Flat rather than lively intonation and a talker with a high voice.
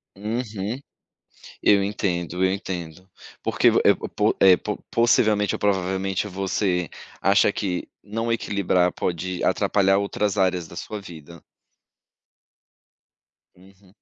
No: narrow, 2.3 semitones; very low, 95 Hz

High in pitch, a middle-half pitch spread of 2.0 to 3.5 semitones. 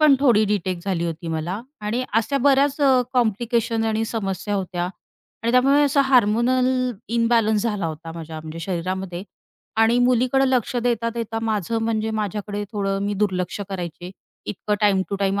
No: high, 215 Hz; average, 4.0 semitones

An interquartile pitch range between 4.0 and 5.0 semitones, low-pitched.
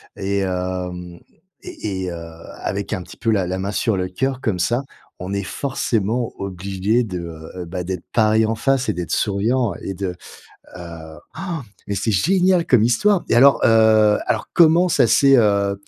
Yes: average, 4.7 semitones; low, 100 Hz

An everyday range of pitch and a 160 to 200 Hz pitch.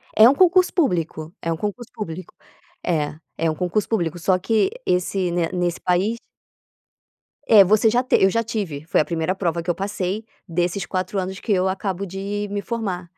Yes: average, 3.3 semitones; high, 190 Hz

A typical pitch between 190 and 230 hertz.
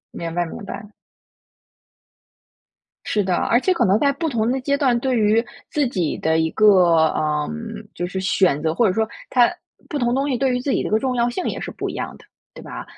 Yes: high, 220 Hz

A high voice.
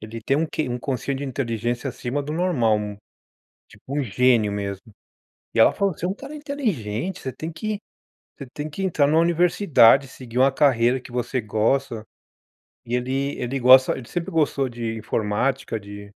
No: low, 130 Hz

